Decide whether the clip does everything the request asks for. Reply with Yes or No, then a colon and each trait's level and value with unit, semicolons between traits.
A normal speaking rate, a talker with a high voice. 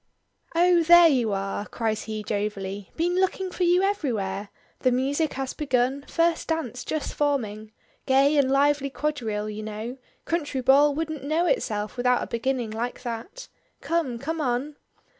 Yes: average, 155 wpm; very high, 270 Hz